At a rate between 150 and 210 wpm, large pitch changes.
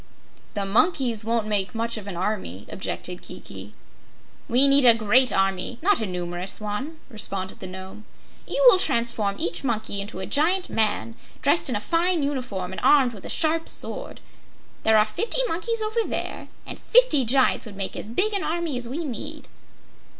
Yes: average, 180 wpm; wide, 7.7 semitones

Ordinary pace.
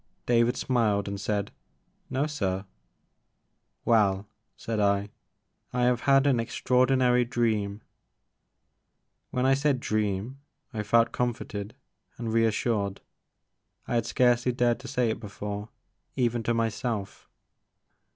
No: slow, 120 wpm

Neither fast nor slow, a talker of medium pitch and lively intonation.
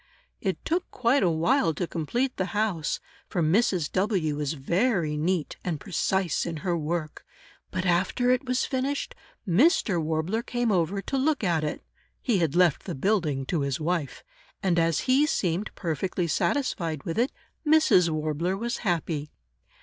Yes: average, 160 wpm; medium, 180 Hz; wide, 6.2 semitones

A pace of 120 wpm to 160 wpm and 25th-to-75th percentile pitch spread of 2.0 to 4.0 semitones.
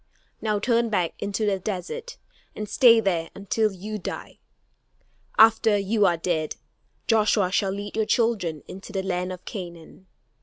Yes: average, 150 wpm; average, 3.0 semitones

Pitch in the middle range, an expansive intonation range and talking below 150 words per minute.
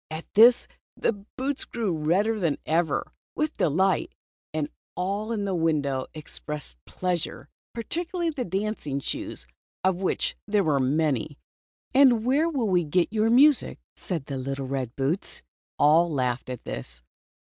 Yes: medium, 175 Hz; wide, 7.2 semitones; average, 140 wpm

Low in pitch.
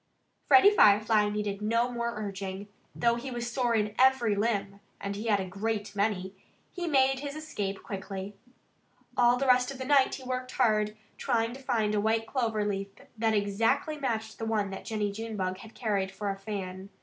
No: high, 220 Hz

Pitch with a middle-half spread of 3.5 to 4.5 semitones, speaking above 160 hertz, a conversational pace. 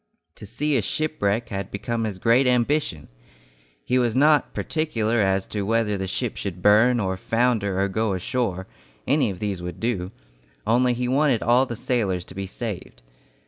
No: average, 4.2 semitones; low, 110 Hz; average, 175 wpm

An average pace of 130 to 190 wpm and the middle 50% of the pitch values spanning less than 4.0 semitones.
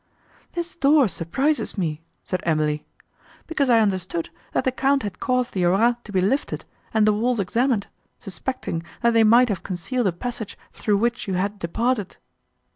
No: average, 170 wpm; average, 5.3 semitones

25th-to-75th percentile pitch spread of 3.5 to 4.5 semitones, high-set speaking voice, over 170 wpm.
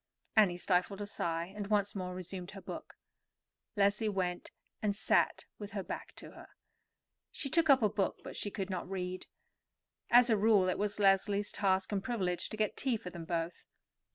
No: narrow, 2.4 semitones; high, 200 Hz; average, 185 wpm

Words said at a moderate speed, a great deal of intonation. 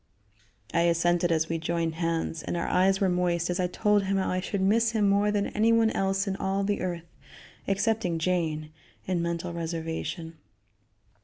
No: average, 175 wpm; average, 2.8 semitones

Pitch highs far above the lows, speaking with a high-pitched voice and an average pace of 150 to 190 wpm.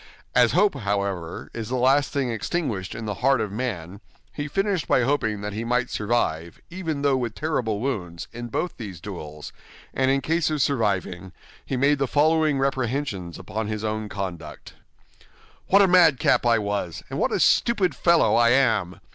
No: wide, 5.8 semitones; low, 120 Hz; average, 175 wpm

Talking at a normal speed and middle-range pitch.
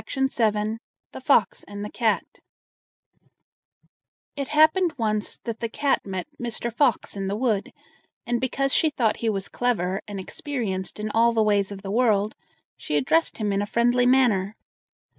No: average, 160 wpm; high, 225 Hz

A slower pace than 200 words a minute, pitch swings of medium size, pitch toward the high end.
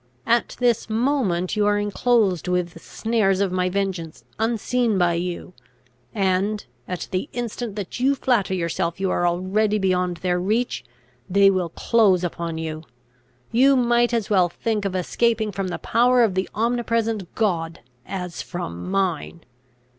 Yes: average, 155 wpm; average, 4.1 semitones; high, 195 Hz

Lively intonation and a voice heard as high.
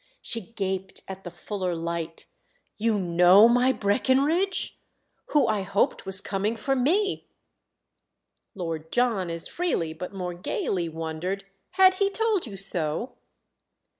Yes: wide, 6.1 semitones; high, 195 Hz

